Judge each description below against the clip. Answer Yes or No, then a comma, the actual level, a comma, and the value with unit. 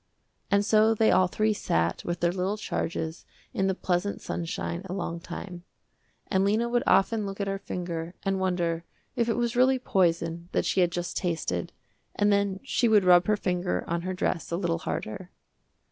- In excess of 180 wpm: Yes, average, 190 wpm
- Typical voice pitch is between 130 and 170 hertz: No, medium, 185 Hz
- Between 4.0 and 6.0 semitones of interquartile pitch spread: No, average, 3.1 semitones